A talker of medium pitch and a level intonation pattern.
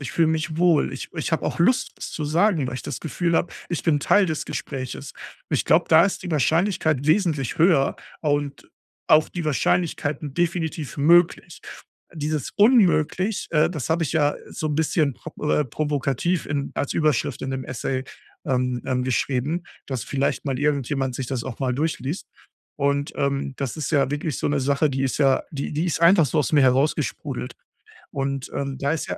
No: medium, 150 Hz; average, 3.2 semitones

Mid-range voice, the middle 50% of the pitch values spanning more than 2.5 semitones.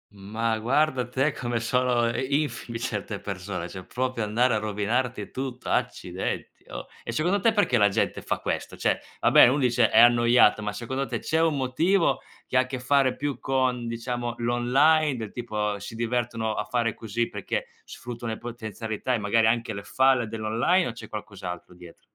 No: low, 120 Hz; average, 2.9 semitones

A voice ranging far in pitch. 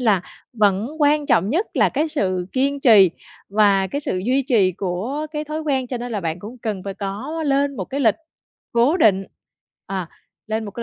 Yes: wide, 6.3 semitones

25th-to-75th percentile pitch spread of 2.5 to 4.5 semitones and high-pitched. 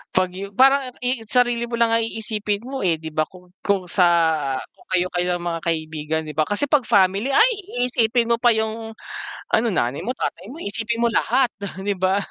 No: average, 5.1 semitones; high, 205 Hz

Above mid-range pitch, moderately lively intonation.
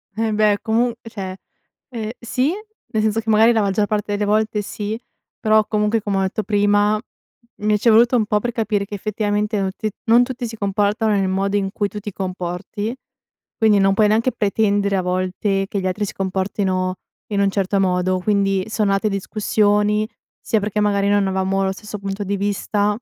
No: high, 205 Hz; narrow, 1.7 semitones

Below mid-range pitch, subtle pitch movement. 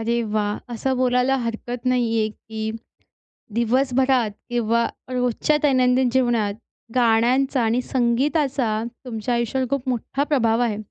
No: high, 245 Hz; narrow, 2.3 semitones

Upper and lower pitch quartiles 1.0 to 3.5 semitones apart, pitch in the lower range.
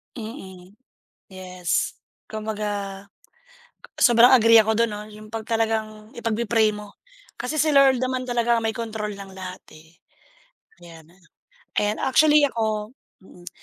No: average, 2.7 semitones; high, 220 Hz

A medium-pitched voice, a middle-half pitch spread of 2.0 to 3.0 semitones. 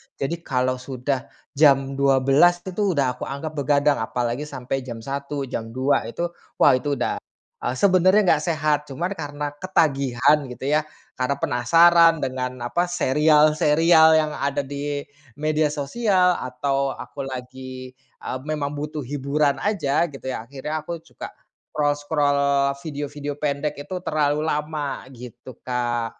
Yes: medium, 145 Hz; narrow, 2.6 semitones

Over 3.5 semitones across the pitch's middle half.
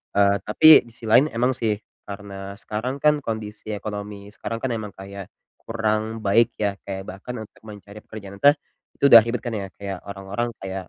No: average, 2.7 semitones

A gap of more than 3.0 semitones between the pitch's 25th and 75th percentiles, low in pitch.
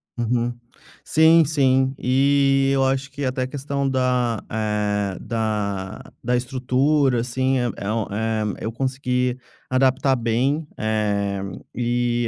No: narrow, 2.6 semitones; low, 125 Hz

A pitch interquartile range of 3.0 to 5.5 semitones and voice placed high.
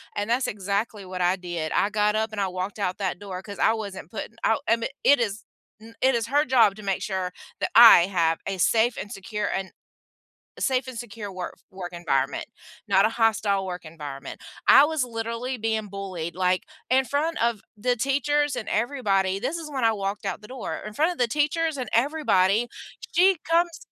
Yes: average, 4.7 semitones; high, 215 Hz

